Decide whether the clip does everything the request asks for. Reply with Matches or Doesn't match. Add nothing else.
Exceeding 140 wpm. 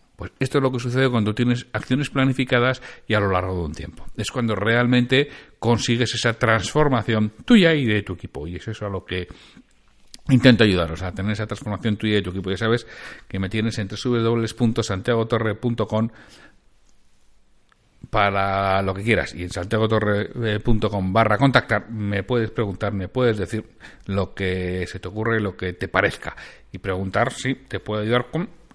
Matches